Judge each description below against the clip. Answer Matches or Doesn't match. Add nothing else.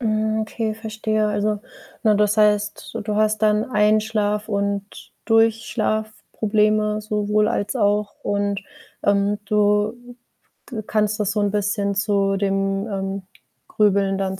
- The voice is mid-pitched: Doesn't match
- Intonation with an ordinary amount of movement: Doesn't match